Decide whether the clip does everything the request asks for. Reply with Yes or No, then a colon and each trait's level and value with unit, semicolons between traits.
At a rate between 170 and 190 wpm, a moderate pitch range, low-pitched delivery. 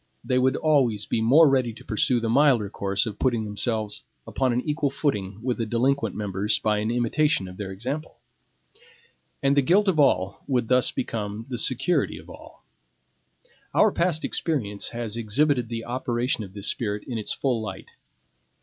Yes: average, 175 wpm; average, 4.4 semitones; low, 120 Hz